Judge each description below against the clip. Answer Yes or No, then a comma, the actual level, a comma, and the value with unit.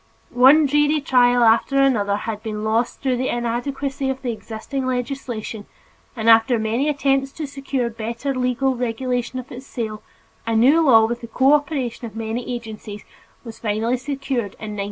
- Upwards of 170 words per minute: No, average, 165 wpm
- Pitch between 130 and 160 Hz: No, high, 245 Hz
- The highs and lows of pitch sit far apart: No, average, 3.2 semitones